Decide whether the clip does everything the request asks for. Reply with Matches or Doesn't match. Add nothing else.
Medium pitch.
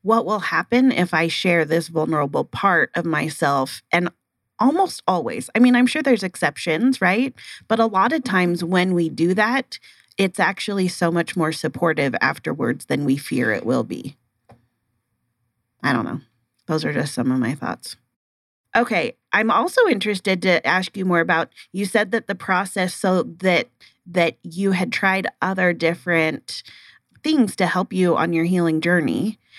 Matches